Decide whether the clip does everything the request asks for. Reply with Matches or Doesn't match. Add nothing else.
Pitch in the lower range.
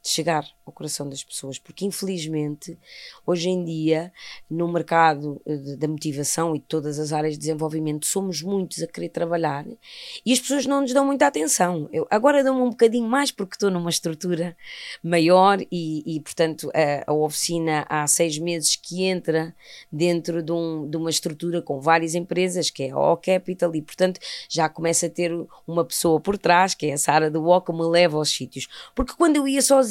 Doesn't match